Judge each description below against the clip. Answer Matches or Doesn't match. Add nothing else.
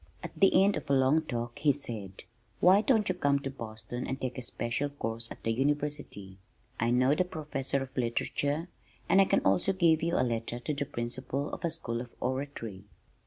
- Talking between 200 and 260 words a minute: Matches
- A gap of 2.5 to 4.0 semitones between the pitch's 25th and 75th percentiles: Doesn't match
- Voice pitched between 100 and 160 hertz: Matches